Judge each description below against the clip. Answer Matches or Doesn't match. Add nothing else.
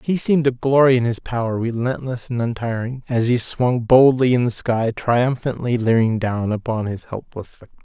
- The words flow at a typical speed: Matches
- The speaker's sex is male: Matches